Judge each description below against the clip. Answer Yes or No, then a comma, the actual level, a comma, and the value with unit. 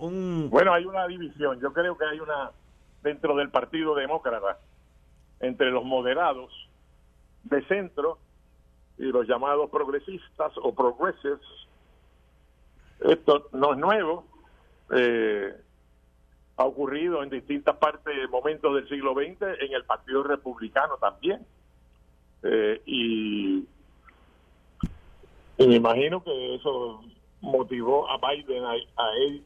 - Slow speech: Yes, slow, 115 wpm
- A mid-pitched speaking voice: No, low, 125 Hz